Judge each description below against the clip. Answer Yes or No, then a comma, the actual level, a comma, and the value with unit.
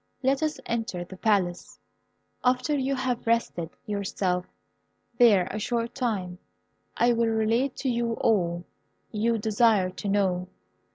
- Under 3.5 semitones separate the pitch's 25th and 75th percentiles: No, average, 4.3 semitones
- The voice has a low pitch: No, high, 220 Hz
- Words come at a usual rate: No, slow, 130 wpm